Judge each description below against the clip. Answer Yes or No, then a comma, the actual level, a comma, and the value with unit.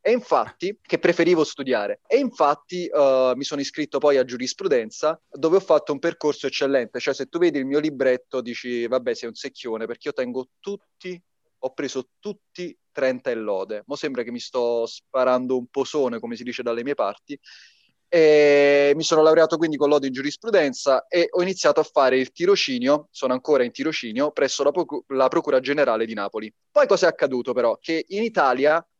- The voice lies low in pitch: No, medium, 145 Hz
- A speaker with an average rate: No, fast, 190 wpm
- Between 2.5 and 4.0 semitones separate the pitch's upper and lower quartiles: No, average, 4.6 semitones